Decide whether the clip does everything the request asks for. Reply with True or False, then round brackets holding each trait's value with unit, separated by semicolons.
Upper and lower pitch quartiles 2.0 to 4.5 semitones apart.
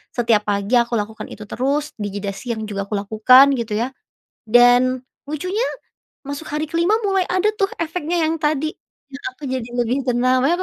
False (5.1 semitones)